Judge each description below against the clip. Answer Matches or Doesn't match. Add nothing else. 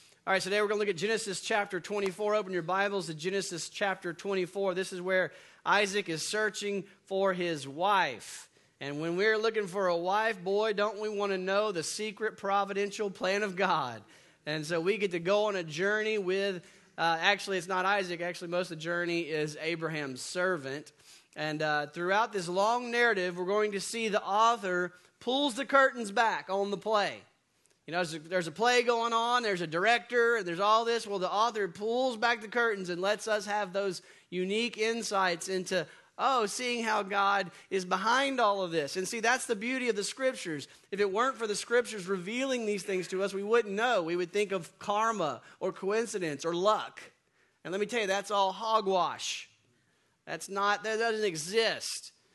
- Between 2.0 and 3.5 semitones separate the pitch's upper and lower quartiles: Matches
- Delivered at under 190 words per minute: Doesn't match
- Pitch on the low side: Doesn't match